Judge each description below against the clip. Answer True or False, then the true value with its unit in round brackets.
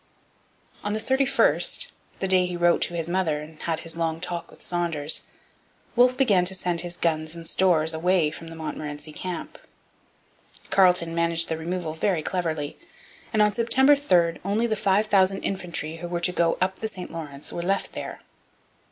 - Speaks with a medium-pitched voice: True (175 Hz)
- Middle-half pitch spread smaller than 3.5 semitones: True (2.8 semitones)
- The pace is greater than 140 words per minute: True (180 wpm)